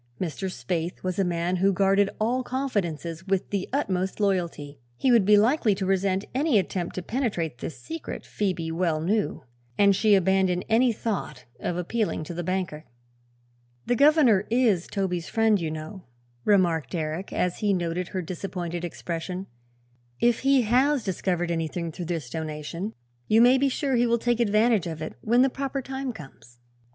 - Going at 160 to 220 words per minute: Yes, average, 170 wpm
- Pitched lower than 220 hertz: Yes, high, 190 Hz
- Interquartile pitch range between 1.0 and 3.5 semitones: No, average, 4.8 semitones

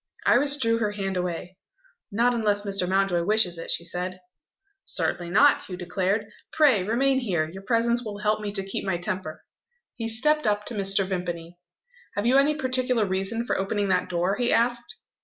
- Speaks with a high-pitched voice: Yes, high, 205 Hz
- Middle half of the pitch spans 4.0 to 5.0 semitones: Yes, average, 4.3 semitones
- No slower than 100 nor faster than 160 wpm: No, average, 180 wpm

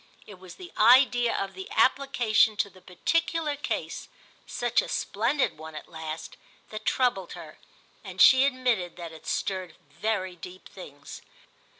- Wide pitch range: Yes, wide, 6.0 semitones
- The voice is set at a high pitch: Yes, high, 205 Hz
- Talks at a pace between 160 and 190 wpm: No, average, 150 wpm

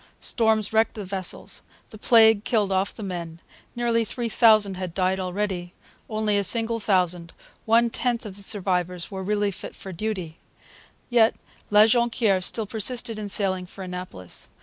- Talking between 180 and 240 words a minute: No, average, 160 wpm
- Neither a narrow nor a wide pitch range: Yes, average, 3.1 semitones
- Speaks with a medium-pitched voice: No, high, 205 Hz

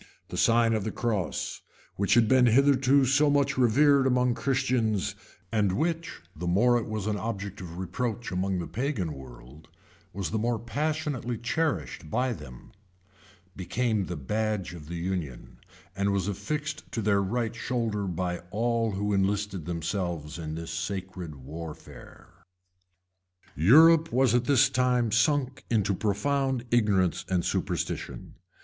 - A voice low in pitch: Yes, low, 110 Hz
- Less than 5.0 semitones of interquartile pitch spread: No, wide, 5.4 semitones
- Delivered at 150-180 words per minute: No, average, 140 wpm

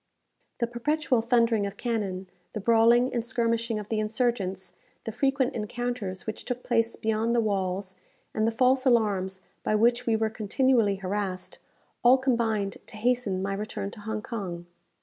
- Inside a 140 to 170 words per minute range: Yes, average, 160 wpm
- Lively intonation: No, average, 3.1 semitones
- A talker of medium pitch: No, high, 225 Hz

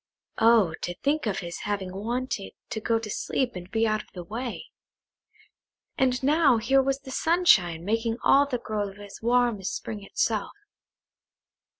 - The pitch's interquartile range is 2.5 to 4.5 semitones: Yes, average, 4.2 semitones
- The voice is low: No, high, 225 Hz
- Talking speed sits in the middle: Yes, average, 165 wpm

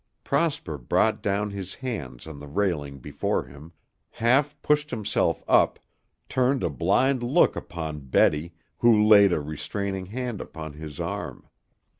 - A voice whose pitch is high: No, low, 100 Hz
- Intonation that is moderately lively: No, wide, 7.8 semitones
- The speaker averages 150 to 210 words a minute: No, average, 140 wpm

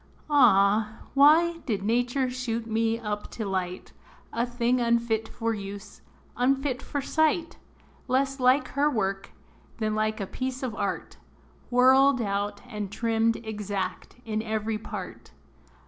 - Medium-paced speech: No, slow, 130 wpm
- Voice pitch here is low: No, high, 230 Hz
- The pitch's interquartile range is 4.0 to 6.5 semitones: No, average, 3.5 semitones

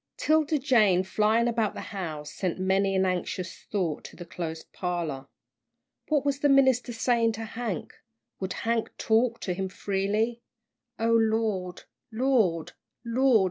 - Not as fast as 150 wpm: Yes, average, 140 wpm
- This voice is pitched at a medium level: No, high, 215 Hz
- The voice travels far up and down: No, average, 4.3 semitones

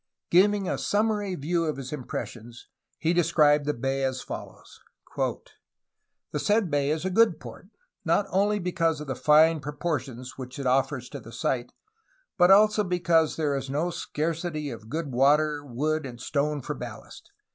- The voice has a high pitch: No, medium, 150 Hz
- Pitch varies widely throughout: No, average, 4.4 semitones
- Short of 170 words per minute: No, average, 175 wpm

